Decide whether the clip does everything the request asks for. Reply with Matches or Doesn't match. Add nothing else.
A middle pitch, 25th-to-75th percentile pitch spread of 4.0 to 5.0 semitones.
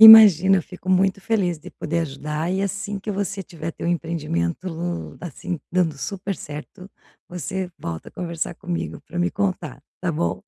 Doesn't match